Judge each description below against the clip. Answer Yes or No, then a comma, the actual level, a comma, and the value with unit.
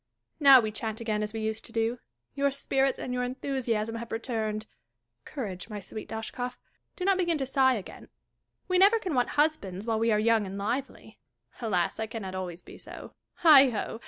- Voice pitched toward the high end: Yes, high, 230 Hz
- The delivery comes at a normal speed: Yes, average, 190 wpm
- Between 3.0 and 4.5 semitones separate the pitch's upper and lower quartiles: Yes, average, 3.8 semitones